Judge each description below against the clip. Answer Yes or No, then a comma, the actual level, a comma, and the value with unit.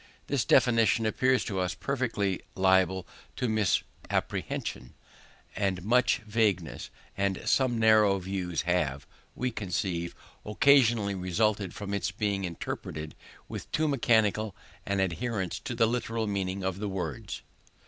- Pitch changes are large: No, average, 3.5 semitones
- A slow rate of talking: Yes, slow, 125 wpm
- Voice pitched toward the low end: Yes, low, 100 Hz